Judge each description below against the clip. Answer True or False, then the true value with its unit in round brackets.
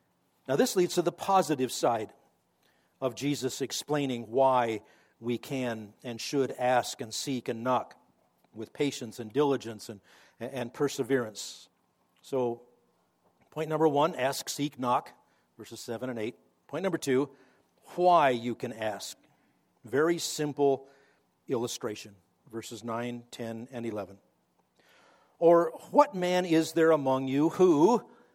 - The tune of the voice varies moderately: True (4.0 semitones)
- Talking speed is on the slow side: True (130 wpm)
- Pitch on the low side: True (130 Hz)